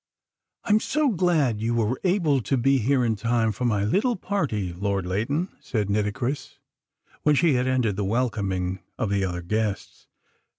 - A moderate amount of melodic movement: No, wide, 5.7 semitones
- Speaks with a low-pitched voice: Yes, low, 115 Hz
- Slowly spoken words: No, average, 165 wpm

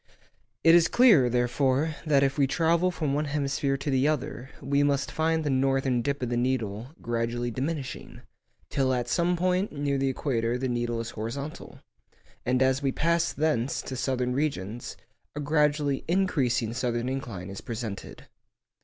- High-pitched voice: No, low, 135 Hz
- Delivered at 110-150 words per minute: No, average, 160 wpm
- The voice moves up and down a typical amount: Yes, average, 3.5 semitones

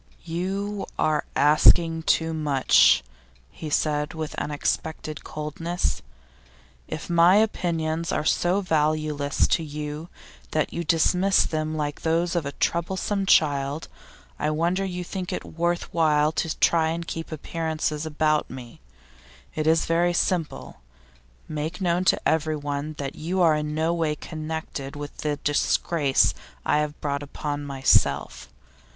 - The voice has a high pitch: No, medium, 155 Hz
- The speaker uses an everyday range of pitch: No, narrow, 2.3 semitones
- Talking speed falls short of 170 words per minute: Yes, slow, 135 wpm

